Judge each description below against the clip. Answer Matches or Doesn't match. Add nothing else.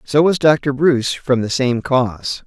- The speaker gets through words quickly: Doesn't match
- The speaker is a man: Matches